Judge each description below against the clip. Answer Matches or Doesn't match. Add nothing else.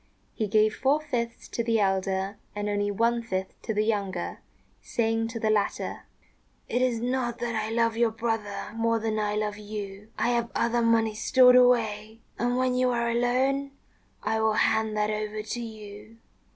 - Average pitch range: Doesn't match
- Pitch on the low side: Doesn't match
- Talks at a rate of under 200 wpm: Matches